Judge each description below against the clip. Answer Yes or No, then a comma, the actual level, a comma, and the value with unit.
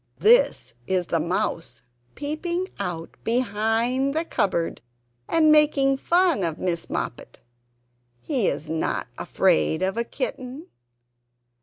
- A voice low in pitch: No, high, 240 Hz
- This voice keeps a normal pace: No, slow, 115 wpm